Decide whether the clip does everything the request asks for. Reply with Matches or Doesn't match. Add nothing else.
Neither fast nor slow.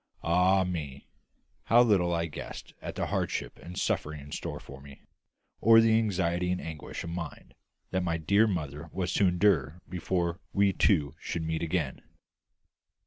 Matches